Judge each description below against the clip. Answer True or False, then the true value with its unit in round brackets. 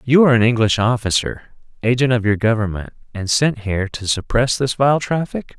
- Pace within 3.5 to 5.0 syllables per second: False (5.4 syllables/s)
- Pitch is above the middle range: False (120 Hz)